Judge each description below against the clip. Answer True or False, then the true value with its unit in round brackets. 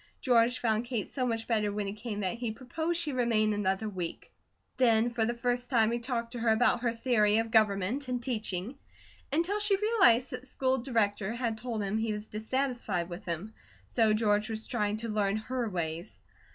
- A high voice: True (225 Hz)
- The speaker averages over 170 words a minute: True (200 wpm)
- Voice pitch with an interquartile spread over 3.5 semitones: False (2.8 semitones)